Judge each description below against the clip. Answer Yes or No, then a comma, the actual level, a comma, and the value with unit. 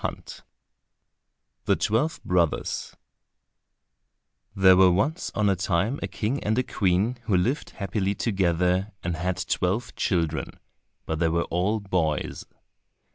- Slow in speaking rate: Yes, slow, 130 wpm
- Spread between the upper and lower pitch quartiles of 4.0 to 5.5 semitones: No, average, 3.4 semitones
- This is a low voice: Yes, very low, 95 Hz